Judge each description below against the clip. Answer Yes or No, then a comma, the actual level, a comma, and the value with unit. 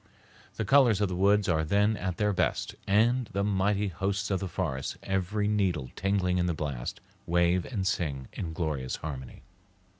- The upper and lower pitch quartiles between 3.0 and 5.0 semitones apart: Yes, average, 3.6 semitones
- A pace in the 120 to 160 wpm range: No, average, 175 wpm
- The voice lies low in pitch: Yes, very low, 95 Hz